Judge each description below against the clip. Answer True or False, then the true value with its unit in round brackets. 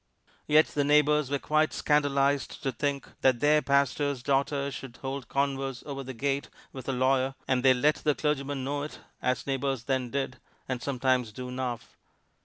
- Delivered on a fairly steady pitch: True (1.7 semitones)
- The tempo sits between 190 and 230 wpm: False (175 wpm)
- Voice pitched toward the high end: False (135 Hz)